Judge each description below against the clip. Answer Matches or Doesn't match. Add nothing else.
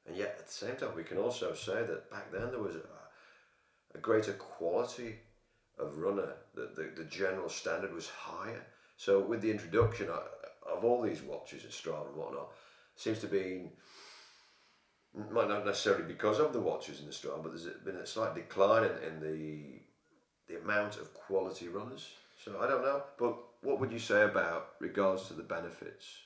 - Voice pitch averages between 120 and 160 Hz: Doesn't match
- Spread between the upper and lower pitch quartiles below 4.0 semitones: Doesn't match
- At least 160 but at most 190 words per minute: Matches